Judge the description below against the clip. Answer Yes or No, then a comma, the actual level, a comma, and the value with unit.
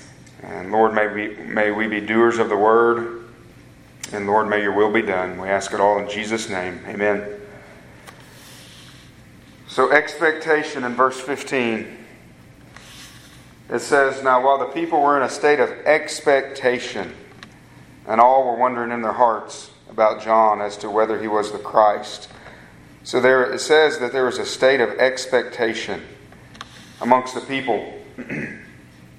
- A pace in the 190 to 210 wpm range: No, average, 150 wpm